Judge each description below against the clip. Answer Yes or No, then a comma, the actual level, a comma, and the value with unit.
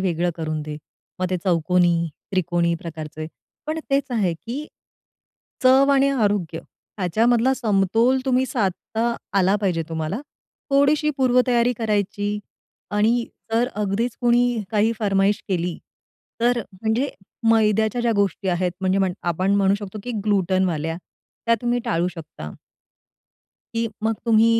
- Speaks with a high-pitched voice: Yes, high, 205 Hz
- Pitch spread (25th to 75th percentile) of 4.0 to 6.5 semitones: Yes, average, 4.9 semitones